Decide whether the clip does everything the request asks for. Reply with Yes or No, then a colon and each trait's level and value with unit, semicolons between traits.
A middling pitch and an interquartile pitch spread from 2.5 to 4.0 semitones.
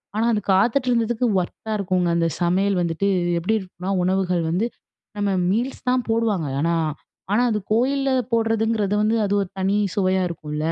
No: high, 200 Hz; average, 3.7 semitones